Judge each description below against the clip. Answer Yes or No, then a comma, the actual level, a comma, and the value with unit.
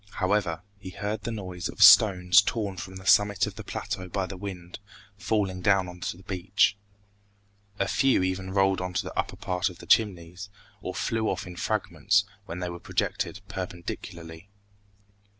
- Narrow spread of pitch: Yes, narrow, 2.2 semitones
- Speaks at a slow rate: No, average, 175 wpm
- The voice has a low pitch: Yes, very low, 95 Hz